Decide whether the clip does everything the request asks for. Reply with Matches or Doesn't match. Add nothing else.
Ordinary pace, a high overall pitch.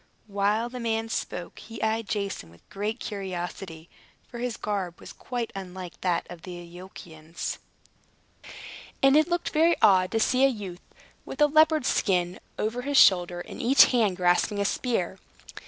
Matches